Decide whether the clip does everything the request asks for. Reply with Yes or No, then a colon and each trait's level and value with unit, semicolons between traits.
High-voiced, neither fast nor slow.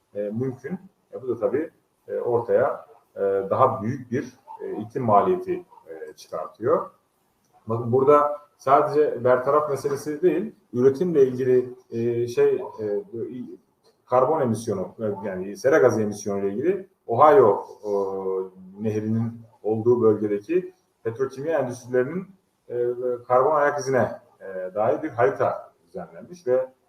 No: low, 135 Hz; average, 120 wpm